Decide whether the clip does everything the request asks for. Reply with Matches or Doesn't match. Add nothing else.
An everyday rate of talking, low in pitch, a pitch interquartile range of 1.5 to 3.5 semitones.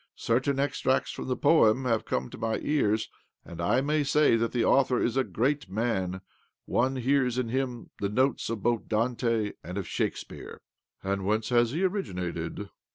Doesn't match